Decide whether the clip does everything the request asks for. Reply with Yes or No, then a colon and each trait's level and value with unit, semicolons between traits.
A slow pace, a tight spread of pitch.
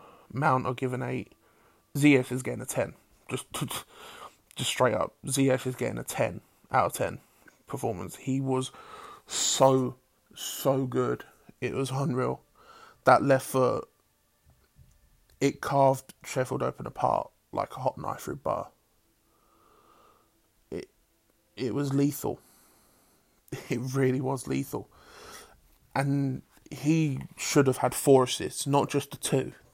Yes: slow, 125 wpm; narrow, 1.6 semitones